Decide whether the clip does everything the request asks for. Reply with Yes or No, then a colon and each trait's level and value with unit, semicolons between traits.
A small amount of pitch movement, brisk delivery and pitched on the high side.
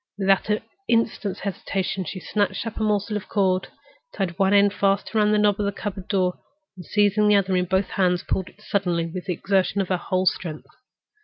Yes: narrow, 2.0 semitones; fast, 215 wpm; high, 195 Hz